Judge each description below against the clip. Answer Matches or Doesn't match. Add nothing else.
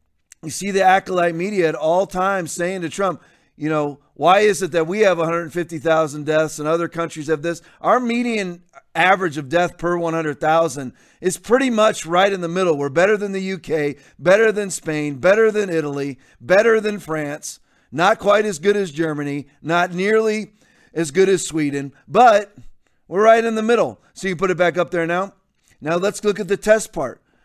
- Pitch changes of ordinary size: Matches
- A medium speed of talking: Matches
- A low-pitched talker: Doesn't match